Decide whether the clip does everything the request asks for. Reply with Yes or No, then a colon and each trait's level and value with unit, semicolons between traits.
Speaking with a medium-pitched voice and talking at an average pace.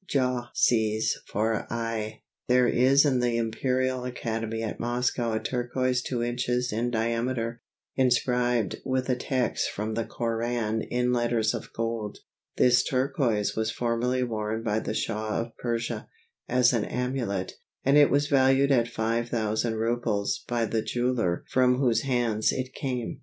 No: low, 120 Hz; average, 145 wpm